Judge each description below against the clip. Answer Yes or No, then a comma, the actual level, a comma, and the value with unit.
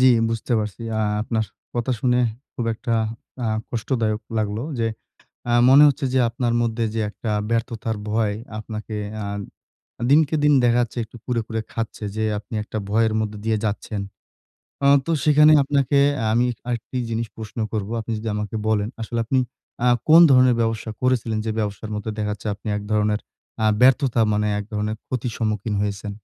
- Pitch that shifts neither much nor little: No, narrow, 2.3 semitones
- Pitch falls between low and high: No, low, 115 Hz